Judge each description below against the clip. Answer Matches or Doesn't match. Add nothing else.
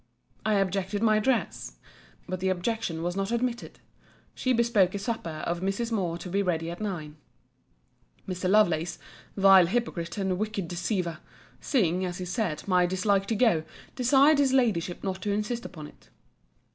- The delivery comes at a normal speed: Matches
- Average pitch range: Matches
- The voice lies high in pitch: Matches